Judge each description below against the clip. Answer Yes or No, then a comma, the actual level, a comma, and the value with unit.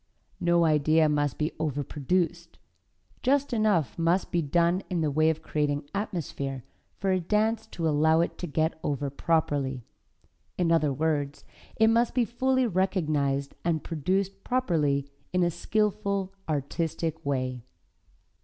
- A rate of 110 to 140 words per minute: Yes, slow, 135 wpm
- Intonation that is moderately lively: Yes, average, 4.6 semitones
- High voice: No, medium, 165 Hz